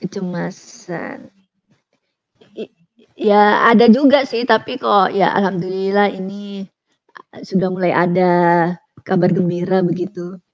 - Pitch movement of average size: No, narrow, 2.1 semitones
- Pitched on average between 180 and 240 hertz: Yes, high, 190 Hz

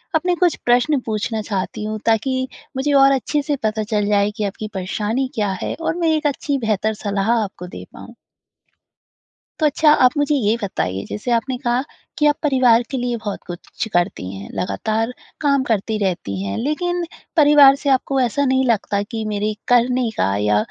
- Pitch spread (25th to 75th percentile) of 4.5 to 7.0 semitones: Yes, average, 5.0 semitones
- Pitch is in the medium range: No, high, 230 Hz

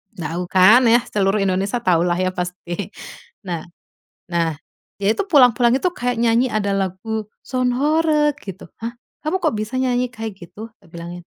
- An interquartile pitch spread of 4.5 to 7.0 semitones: Yes, average, 5.2 semitones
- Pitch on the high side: Yes, high, 215 Hz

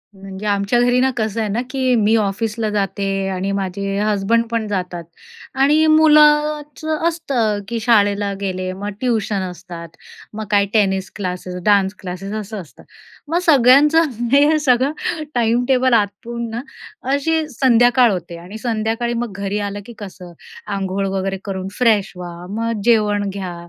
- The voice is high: Yes, high, 215 Hz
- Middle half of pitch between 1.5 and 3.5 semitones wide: No, average, 3.9 semitones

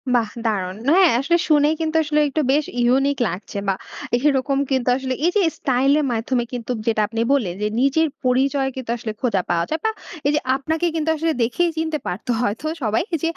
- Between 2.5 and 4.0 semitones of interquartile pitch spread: No, average, 5.0 semitones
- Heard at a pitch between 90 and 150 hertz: No, very high, 265 Hz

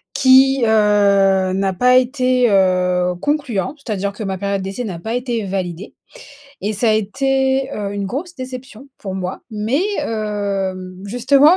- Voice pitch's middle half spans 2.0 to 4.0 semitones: No, average, 4.8 semitones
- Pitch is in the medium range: No, high, 210 Hz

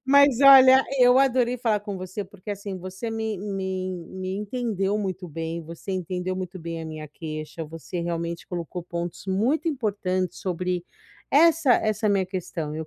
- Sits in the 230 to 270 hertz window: No, high, 190 Hz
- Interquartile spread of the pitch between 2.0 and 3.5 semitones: No, average, 4.4 semitones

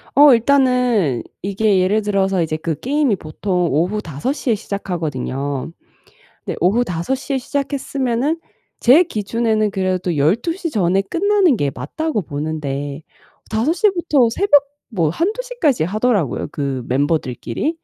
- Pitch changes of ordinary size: No, wide, 9.0 semitones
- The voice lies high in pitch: Yes, high, 210 Hz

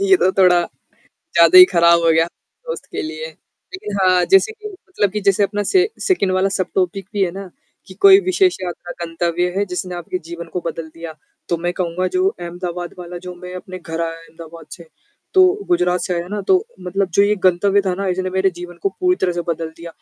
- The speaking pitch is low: No, medium, 185 Hz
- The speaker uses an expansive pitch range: No, average, 2.9 semitones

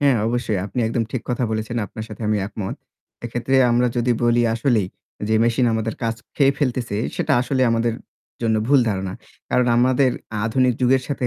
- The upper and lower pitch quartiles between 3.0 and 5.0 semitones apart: No, narrow, 2.4 semitones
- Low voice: Yes, low, 120 Hz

